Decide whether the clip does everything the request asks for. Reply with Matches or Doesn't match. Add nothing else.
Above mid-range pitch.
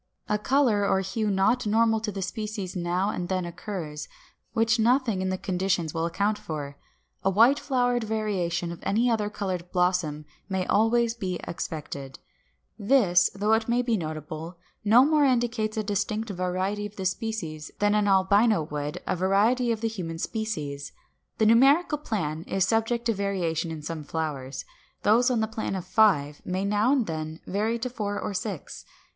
Matches